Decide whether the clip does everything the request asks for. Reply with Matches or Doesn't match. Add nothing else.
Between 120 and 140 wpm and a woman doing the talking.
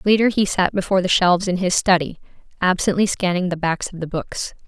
Doesn't match